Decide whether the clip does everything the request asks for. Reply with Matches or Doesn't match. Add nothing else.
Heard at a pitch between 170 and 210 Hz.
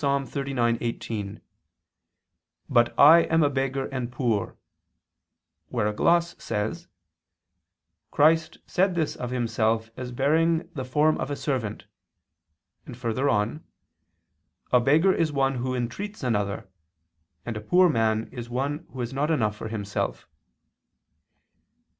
Doesn't match